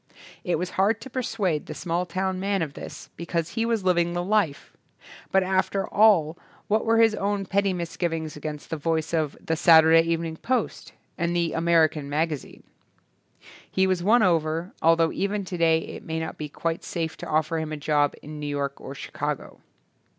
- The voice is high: No, medium, 170 Hz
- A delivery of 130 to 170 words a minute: No, average, 180 wpm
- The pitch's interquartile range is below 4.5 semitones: Yes, average, 3.3 semitones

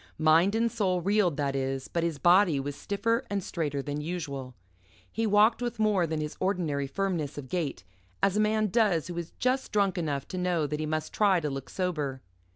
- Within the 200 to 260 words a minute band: Yes, fast, 205 wpm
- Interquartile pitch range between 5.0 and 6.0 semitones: Yes, wide, 5.6 semitones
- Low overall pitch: No, medium, 175 Hz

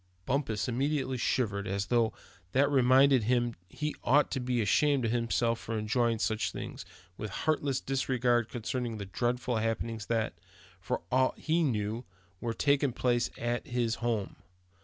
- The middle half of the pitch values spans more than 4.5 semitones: No, average, 2.7 semitones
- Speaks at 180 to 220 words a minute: No, average, 155 wpm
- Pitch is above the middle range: No, low, 120 Hz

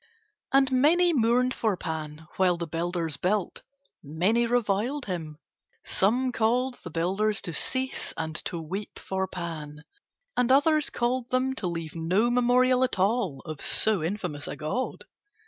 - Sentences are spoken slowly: No, average, 145 wpm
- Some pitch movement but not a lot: No, wide, 7.0 semitones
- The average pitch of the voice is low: No, high, 205 Hz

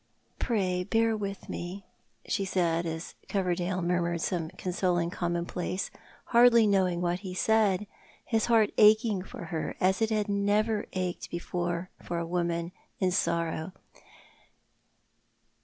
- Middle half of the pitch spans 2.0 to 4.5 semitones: Yes, average, 3.0 semitones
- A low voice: No, medium, 185 Hz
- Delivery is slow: Yes, slow, 125 wpm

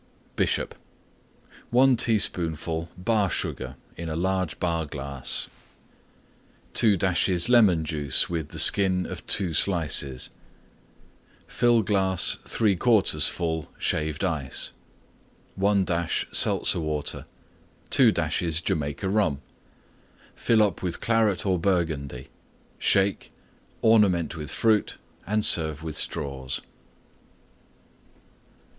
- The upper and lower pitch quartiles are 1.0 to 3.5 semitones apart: No, average, 4.3 semitones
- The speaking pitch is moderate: No, very low, 85 Hz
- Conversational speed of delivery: No, slow, 100 wpm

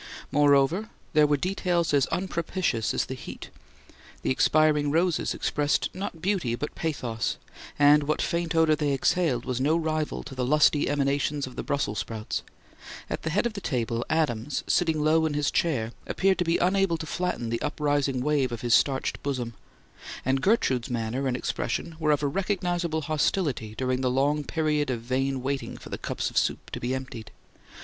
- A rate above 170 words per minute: Yes, average, 180 wpm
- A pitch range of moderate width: Yes, average, 3.8 semitones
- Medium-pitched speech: Yes, medium, 145 Hz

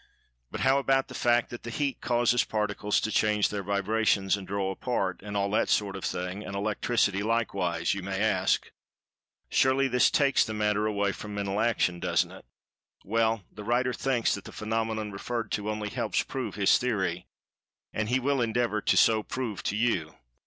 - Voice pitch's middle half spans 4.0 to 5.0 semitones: No, average, 3.1 semitones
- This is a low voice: Yes, low, 105 Hz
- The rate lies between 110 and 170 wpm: No, average, 185 wpm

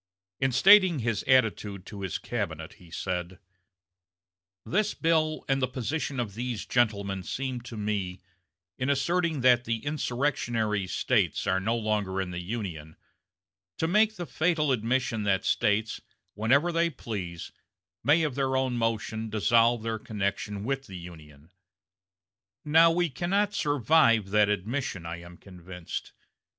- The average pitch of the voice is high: No, low, 115 Hz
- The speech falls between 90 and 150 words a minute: Yes, average, 140 wpm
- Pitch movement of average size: No, wide, 6.0 semitones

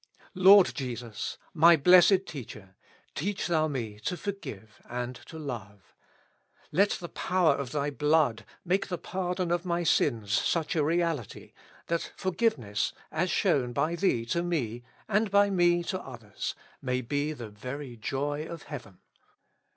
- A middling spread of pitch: No, wide, 6.2 semitones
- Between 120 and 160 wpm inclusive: Yes, average, 150 wpm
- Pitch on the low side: No, medium, 150 Hz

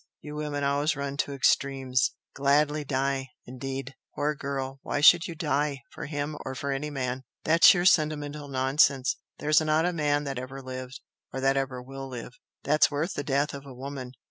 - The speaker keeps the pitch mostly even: Yes, narrow, 1.9 semitones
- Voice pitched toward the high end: No, medium, 140 Hz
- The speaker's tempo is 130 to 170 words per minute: No, average, 185 wpm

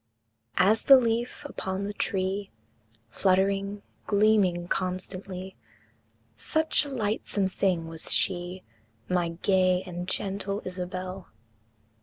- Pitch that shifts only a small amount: Yes, narrow, 1.8 semitones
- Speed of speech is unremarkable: No, slow, 100 wpm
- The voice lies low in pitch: No, high, 190 Hz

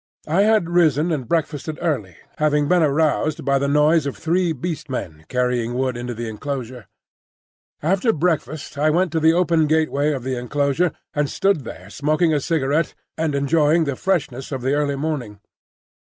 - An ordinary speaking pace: Yes, average, 170 wpm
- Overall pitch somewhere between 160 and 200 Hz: No, medium, 150 Hz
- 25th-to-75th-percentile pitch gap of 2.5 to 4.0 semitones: Yes, average, 3.6 semitones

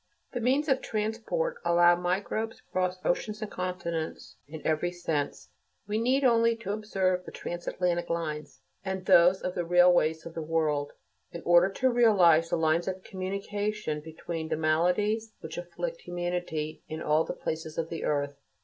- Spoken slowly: No, average, 160 wpm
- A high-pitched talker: No, medium, 175 Hz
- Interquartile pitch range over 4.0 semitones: Yes, average, 4.4 semitones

